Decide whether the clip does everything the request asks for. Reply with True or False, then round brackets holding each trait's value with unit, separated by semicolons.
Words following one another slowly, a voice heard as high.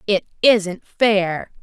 True (110 wpm; 200 Hz)